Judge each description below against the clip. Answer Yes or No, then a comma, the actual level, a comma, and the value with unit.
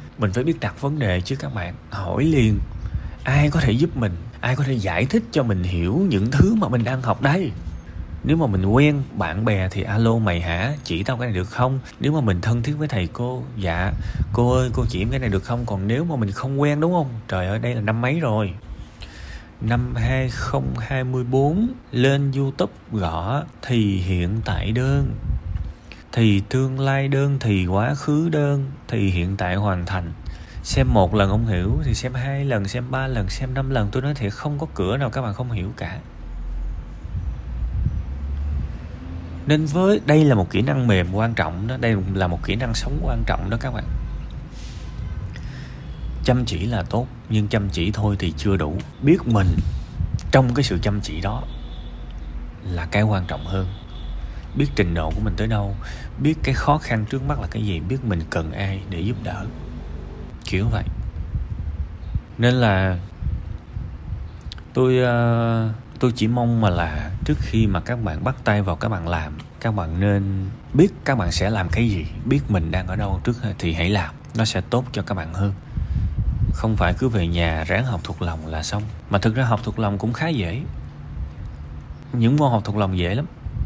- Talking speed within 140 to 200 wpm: Yes, average, 195 wpm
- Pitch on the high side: No, low, 105 Hz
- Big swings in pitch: Yes, wide, 5.8 semitones